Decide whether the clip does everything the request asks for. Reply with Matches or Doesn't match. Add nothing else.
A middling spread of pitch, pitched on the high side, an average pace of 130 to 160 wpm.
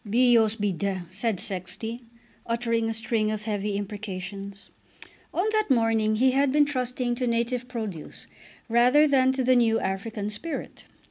Matches